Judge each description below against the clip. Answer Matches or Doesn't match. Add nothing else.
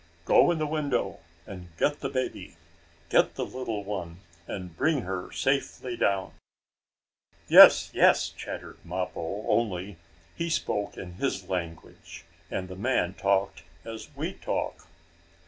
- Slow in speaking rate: Matches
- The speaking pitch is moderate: Doesn't match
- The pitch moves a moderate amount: Doesn't match